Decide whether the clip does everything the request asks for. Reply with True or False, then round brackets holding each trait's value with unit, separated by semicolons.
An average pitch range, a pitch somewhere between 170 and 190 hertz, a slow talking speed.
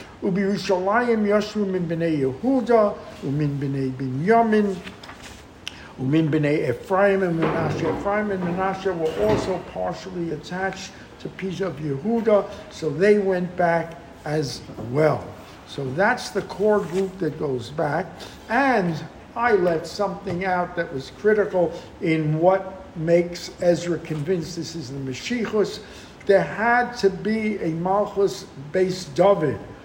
True (4.4 semitones; 185 Hz; 120 wpm)